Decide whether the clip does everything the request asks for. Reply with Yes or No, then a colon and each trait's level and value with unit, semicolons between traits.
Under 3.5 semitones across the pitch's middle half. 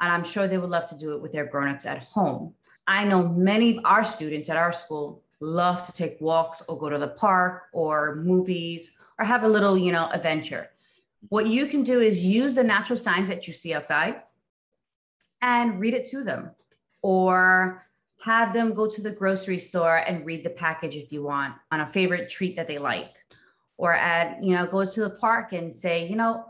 No: average, 4.6 semitones